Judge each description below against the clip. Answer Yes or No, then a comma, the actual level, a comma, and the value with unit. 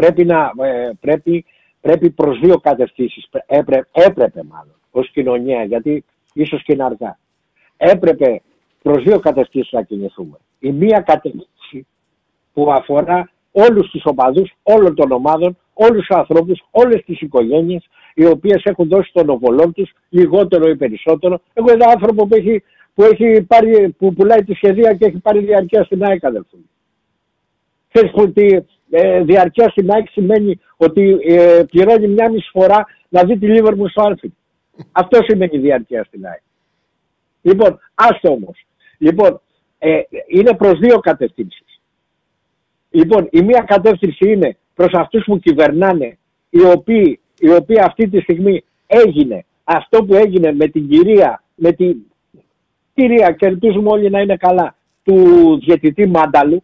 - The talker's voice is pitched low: No, medium, 185 Hz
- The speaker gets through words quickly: No, average, 145 wpm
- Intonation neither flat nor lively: Yes, average, 4.9 semitones